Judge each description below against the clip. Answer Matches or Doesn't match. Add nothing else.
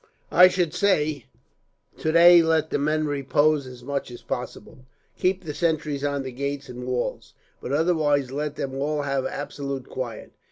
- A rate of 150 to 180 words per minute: Matches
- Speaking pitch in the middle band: Matches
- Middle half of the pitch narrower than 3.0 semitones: Matches